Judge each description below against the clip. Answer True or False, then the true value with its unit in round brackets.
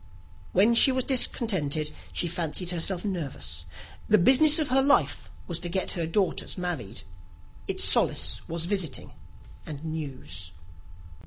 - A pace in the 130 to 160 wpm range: True (135 wpm)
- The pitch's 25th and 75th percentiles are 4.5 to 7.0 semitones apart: True (5.6 semitones)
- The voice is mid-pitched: True (175 Hz)